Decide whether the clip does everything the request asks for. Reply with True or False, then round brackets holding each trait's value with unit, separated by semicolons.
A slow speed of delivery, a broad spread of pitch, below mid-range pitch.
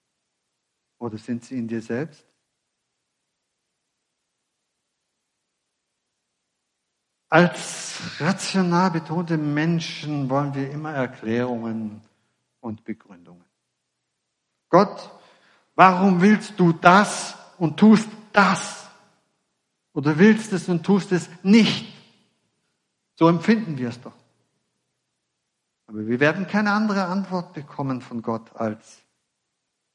False (95 wpm; 8.0 semitones; 165 Hz)